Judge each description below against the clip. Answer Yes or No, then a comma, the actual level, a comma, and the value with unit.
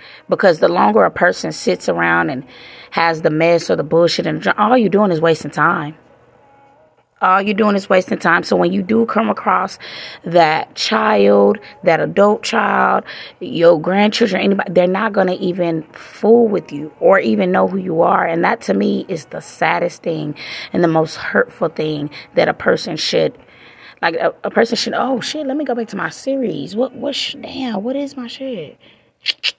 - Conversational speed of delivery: Yes, average, 190 wpm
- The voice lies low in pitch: No, medium, 185 Hz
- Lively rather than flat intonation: Yes, wide, 6.3 semitones